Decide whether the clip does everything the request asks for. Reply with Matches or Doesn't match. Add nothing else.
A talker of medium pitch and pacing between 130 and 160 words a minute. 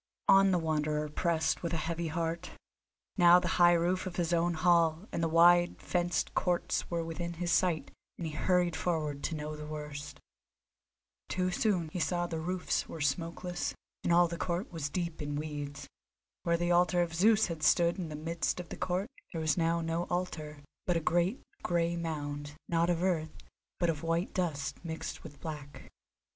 Doesn't match